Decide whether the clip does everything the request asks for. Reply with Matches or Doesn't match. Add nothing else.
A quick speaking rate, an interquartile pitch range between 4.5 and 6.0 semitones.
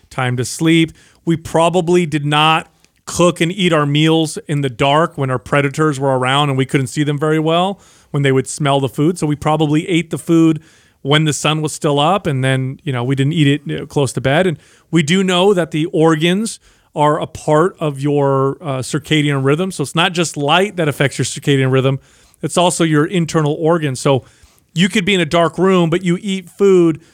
Doesn't match